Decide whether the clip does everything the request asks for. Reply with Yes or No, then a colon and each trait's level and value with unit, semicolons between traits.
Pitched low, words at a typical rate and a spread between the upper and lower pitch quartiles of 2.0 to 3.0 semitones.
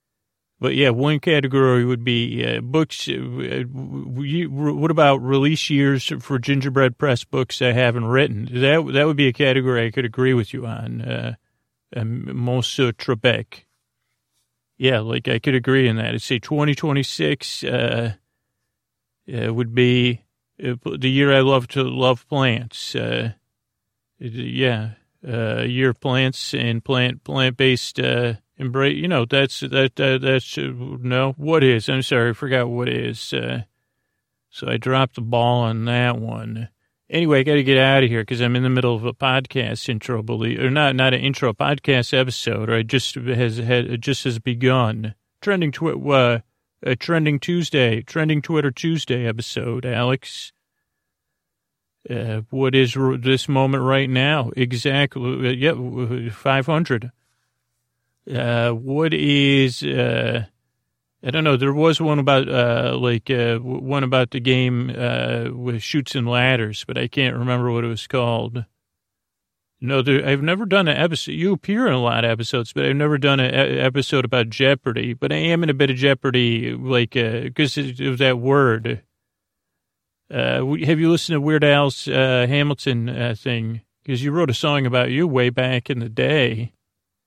Yes: low, 125 Hz; average, 170 wpm; average, 2.7 semitones